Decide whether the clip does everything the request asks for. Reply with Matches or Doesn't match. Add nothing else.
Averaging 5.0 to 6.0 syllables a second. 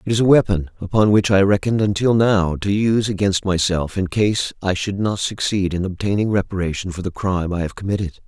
Matches